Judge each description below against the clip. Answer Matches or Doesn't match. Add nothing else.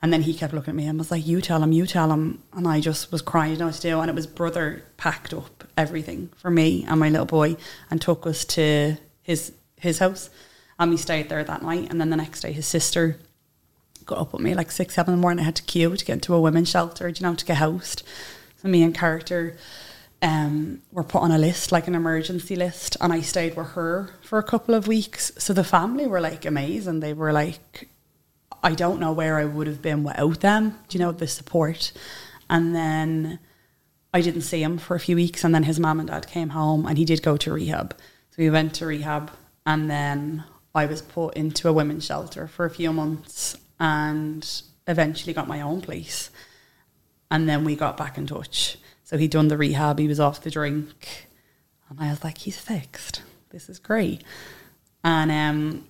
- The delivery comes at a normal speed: Doesn't match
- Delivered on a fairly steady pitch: Matches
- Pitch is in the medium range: Matches